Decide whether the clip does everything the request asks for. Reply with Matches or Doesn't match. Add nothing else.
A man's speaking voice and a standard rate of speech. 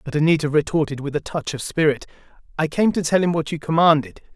Doesn't match